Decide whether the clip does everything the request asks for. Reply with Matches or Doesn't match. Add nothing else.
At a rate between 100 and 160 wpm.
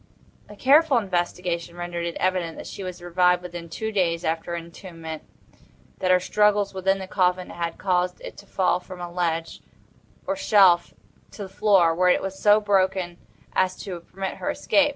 Doesn't match